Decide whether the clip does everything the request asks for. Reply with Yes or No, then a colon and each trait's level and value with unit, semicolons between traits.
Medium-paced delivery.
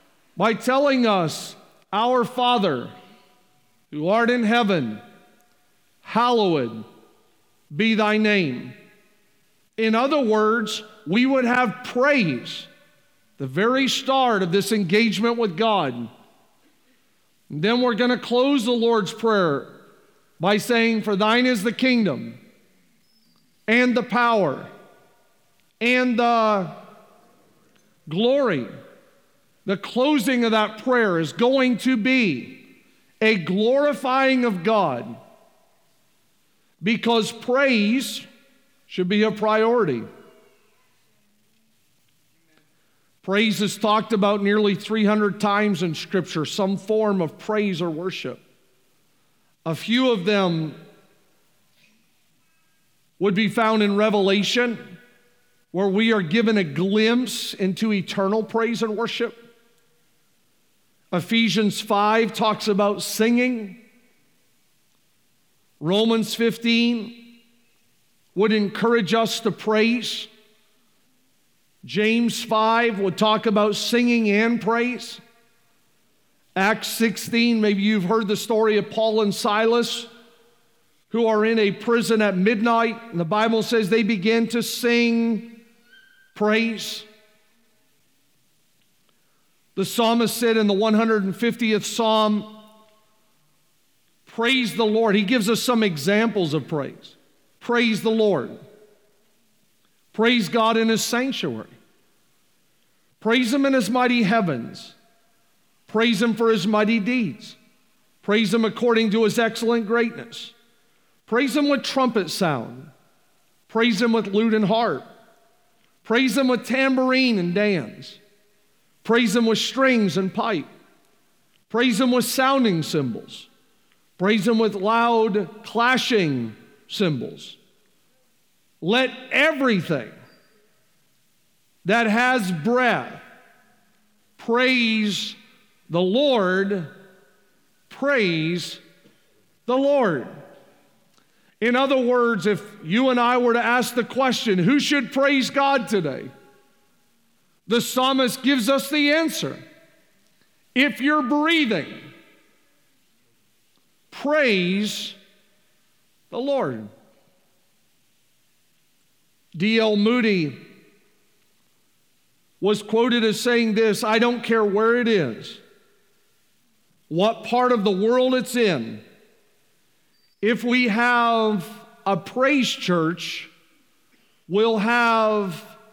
No: slow, 100 wpm